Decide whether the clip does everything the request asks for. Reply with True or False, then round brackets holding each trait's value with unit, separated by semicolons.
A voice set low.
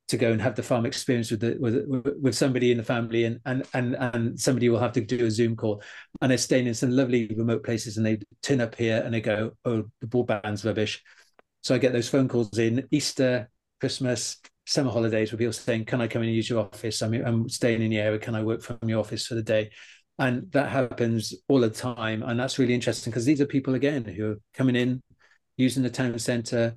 True (120 Hz)